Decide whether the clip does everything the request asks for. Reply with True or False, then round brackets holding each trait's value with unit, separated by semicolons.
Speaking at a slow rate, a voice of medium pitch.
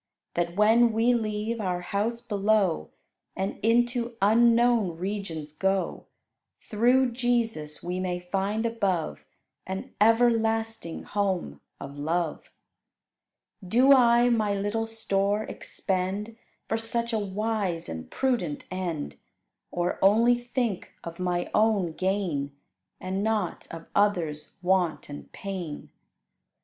False (115 wpm; 205 Hz)